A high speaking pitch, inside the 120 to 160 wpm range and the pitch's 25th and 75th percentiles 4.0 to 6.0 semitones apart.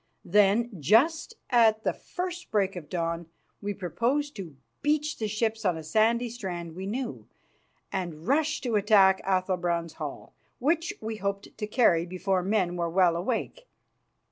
Yes: high, 205 Hz; average, 150 wpm; average, 5.1 semitones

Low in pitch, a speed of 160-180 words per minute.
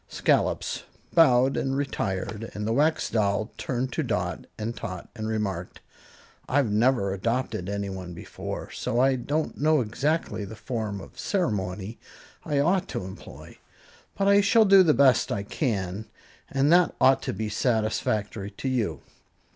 No: low, 115 Hz; average, 150 wpm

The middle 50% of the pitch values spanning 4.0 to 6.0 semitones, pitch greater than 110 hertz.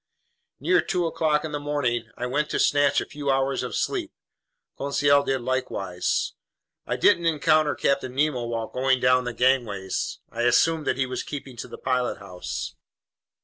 No: average, 3.1 semitones; low, 135 Hz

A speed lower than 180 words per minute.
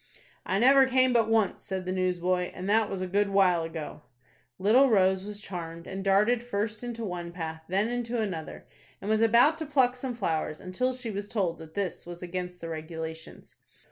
No: average, 195 wpm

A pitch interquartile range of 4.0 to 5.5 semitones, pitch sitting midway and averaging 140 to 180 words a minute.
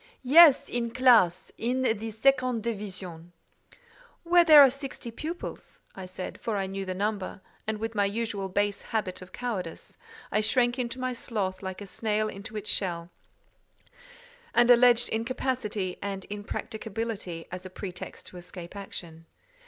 No: average, 4.3 semitones; high, 215 Hz; average, 150 wpm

